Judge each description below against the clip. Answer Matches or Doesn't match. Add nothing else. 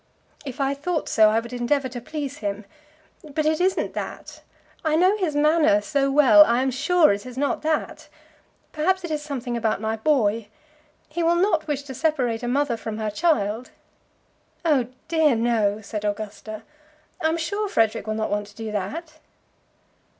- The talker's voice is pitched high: Matches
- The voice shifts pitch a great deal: Matches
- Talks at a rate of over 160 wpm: Matches